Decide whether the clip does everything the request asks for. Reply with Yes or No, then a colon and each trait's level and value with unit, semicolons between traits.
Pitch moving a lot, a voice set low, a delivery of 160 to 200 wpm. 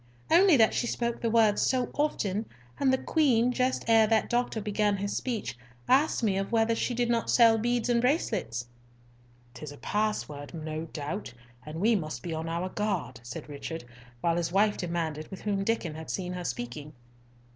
No: wide, 6.4 semitones; high, 205 Hz; average, 185 wpm